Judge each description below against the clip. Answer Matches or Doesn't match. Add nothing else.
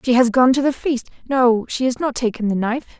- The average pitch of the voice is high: Matches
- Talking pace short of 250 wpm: Doesn't match